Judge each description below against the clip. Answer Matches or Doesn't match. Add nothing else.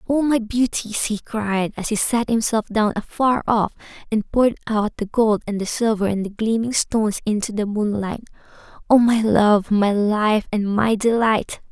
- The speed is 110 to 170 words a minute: Doesn't match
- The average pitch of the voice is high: Matches